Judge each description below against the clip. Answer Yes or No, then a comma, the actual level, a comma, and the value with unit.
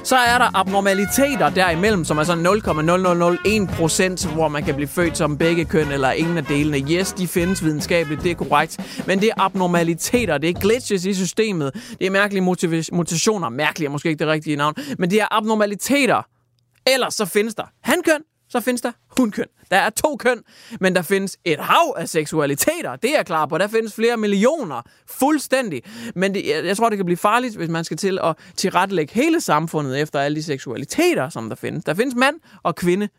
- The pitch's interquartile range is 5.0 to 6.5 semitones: Yes, wide, 5.5 semitones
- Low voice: No, medium, 185 Hz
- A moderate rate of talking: Yes, average, 200 wpm